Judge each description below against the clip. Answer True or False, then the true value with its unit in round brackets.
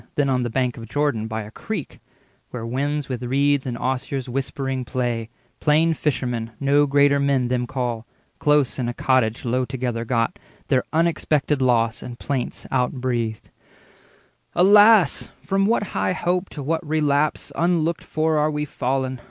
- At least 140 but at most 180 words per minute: True (160 wpm)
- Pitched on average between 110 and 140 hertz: True (135 Hz)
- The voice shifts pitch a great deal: False (3.4 semitones)